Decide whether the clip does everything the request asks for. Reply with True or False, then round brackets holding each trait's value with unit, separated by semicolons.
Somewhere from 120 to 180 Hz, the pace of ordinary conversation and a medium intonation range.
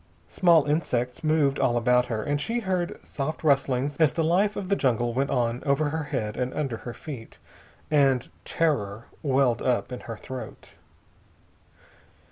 True (140 Hz; 160 wpm; 4.1 semitones)